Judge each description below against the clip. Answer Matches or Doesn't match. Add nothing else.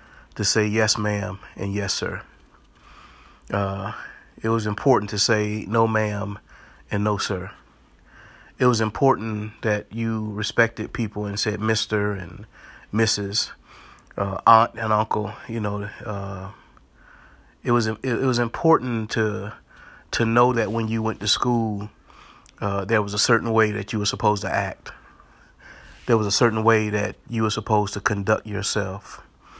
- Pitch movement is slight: Matches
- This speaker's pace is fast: Doesn't match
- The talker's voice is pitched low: Matches